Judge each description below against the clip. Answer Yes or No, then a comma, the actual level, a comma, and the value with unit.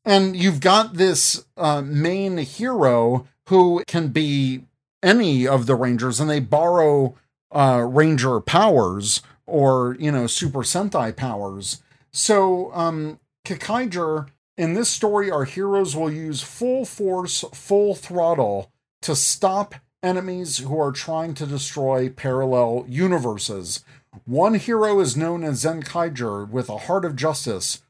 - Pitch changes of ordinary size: No, wide, 5.8 semitones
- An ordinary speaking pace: No, slow, 130 wpm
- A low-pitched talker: No, medium, 150 Hz